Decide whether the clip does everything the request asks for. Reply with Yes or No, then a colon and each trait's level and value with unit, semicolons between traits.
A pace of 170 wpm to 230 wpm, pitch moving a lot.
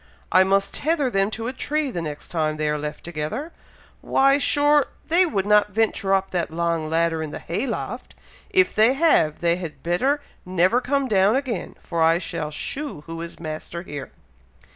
Yes: average, 185 wpm; wide, 8.0 semitones